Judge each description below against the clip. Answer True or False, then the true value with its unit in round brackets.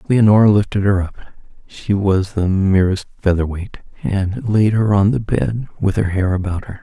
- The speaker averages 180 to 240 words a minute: False (160 wpm)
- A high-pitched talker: False (100 Hz)